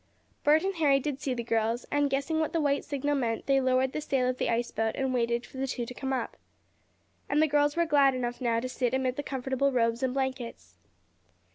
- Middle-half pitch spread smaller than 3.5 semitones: Yes, average, 2.9 semitones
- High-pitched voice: Yes, very high, 265 Hz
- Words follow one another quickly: Yes, fast, 235 wpm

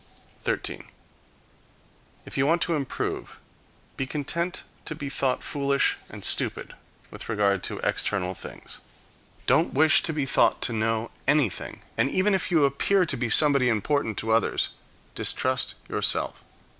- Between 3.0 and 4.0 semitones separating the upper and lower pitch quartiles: No, average, 5.2 semitones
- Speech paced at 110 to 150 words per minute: Yes, average, 145 wpm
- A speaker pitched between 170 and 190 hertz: No, medium, 140 Hz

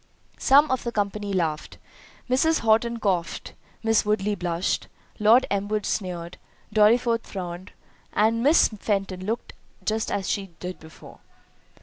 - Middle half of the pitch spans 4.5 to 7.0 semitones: No, average, 3.5 semitones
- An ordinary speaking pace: No, slow, 100 wpm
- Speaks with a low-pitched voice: No, high, 210 Hz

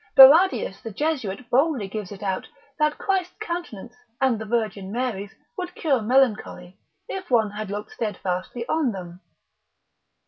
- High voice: Yes, high, 230 Hz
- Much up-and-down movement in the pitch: Yes, wide, 6.8 semitones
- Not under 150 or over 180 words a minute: No, average, 140 wpm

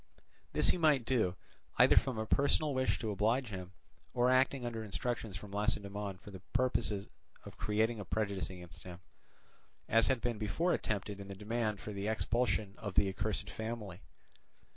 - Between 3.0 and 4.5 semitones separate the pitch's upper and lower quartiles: Yes, average, 3.3 semitones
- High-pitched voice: No, low, 110 Hz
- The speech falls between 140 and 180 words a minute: Yes, average, 170 wpm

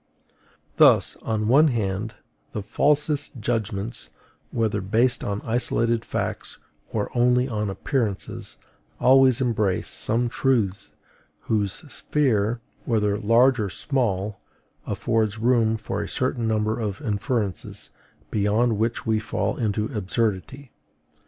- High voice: No, low, 110 Hz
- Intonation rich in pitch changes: No, average, 2.9 semitones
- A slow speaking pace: Yes, slow, 115 wpm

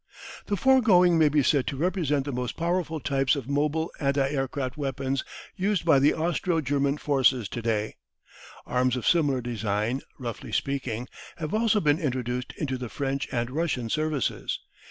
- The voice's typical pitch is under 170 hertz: Yes, medium, 140 Hz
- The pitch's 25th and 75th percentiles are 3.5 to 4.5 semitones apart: Yes, average, 4.0 semitones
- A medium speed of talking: Yes, average, 160 wpm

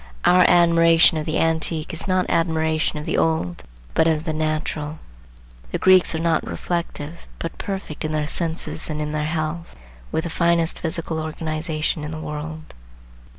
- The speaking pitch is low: No, medium, 160 Hz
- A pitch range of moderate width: No, narrow, 1.3 semitones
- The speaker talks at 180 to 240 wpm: No, average, 165 wpm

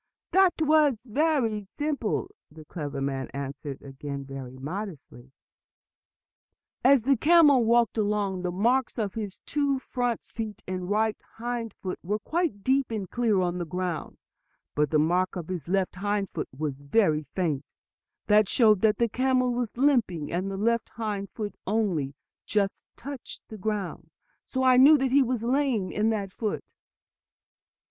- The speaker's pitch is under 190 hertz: No, high, 210 Hz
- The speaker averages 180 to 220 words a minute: No, average, 160 wpm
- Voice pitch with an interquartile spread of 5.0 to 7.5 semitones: Yes, wide, 5.5 semitones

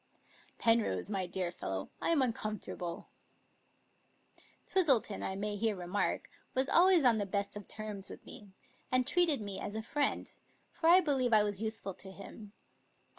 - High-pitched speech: Yes, high, 215 Hz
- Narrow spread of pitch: No, average, 4.7 semitones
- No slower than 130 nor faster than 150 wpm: No, average, 160 wpm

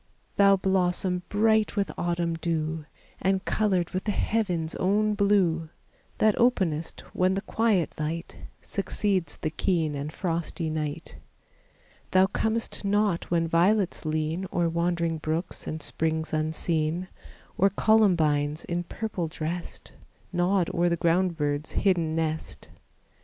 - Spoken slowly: Yes, slow, 125 wpm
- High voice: No, medium, 175 Hz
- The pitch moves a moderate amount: Yes, average, 3.4 semitones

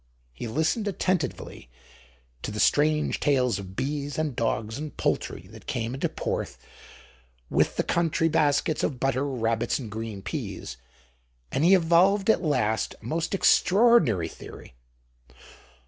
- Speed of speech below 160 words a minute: Yes, slow, 135 wpm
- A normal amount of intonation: No, wide, 6.3 semitones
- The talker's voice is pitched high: No, medium, 145 Hz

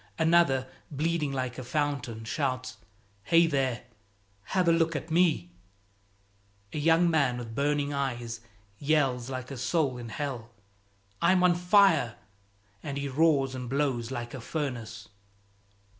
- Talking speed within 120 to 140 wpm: Yes, slow, 135 wpm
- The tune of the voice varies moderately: Yes, average, 4.4 semitones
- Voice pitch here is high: No, medium, 140 Hz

